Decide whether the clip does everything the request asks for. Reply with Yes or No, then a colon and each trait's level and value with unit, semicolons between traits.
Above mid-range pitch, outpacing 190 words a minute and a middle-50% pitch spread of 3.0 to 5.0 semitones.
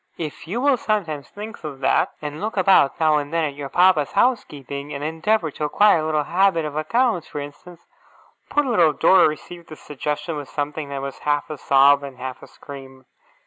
No: medium, 155 Hz; fast, 205 wpm; average, 4.1 semitones